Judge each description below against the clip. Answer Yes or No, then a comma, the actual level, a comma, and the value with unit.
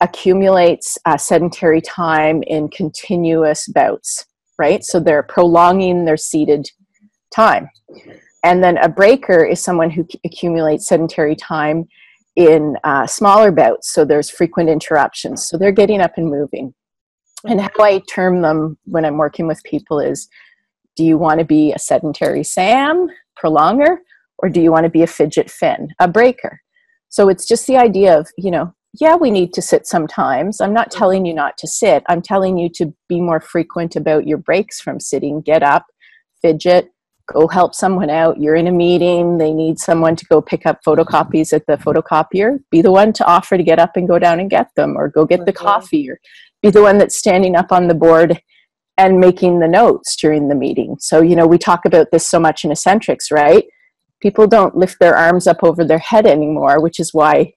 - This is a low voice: No, medium, 175 Hz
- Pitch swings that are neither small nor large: Yes, average, 3.6 semitones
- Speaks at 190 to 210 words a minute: Yes, average, 195 wpm